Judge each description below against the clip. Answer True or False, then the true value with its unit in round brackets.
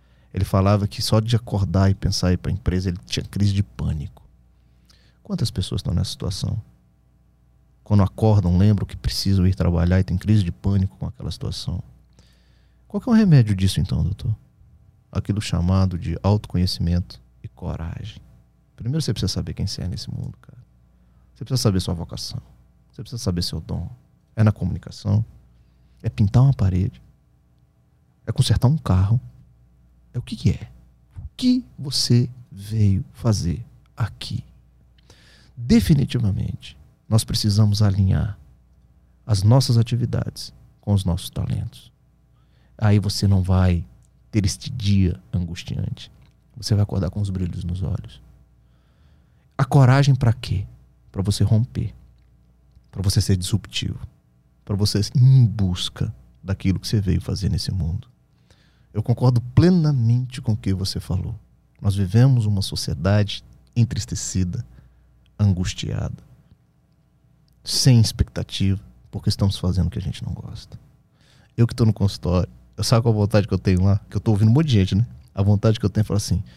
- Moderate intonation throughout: True (4.4 semitones)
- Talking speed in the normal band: True (155 wpm)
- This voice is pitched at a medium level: False (100 Hz)